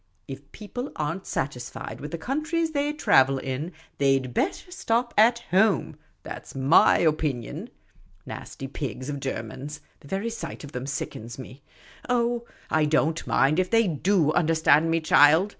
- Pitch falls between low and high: Yes, medium, 155 Hz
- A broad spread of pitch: Yes, wide, 8.3 semitones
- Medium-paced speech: Yes, average, 165 wpm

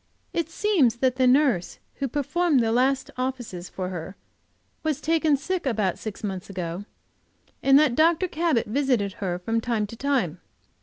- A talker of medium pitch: No, very high, 255 Hz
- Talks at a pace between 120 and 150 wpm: No, average, 160 wpm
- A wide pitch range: Yes, wide, 6.3 semitones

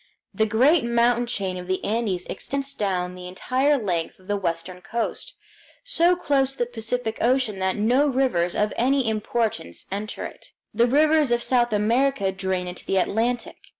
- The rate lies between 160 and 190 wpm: Yes, average, 170 wpm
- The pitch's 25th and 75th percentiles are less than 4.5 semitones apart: No, average, 5.3 semitones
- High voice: Yes, high, 225 Hz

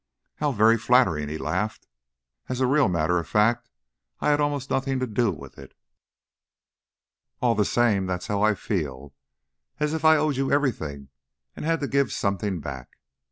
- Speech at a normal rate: Yes, average, 170 wpm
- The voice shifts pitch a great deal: Yes, wide, 7.3 semitones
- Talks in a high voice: No, low, 115 Hz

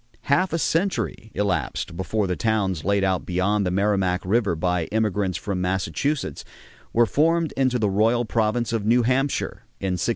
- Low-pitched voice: Yes, low, 105 Hz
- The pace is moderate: Yes, average, 165 wpm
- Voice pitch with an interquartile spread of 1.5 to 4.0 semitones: No, average, 4.6 semitones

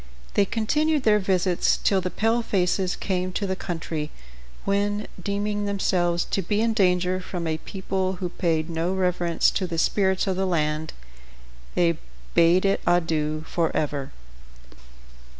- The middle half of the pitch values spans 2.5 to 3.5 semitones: Yes, average, 2.9 semitones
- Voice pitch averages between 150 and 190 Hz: Yes, medium, 185 Hz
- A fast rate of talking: No, average, 140 wpm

